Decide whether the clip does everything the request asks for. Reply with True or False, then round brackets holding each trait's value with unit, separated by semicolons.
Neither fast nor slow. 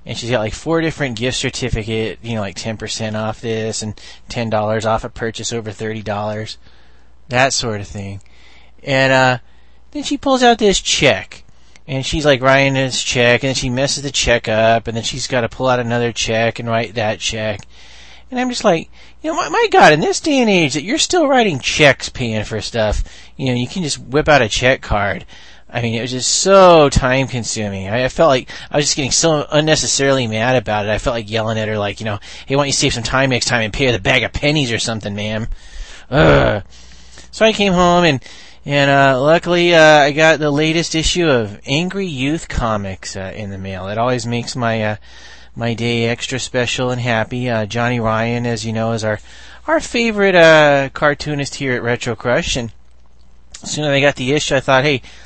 False (220 wpm)